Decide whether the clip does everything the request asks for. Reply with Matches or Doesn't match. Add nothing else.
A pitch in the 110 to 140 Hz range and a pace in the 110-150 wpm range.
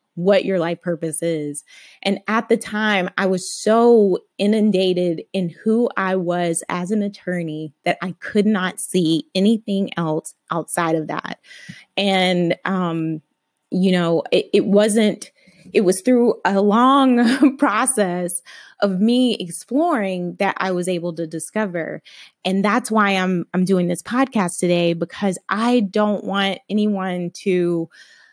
Doesn't match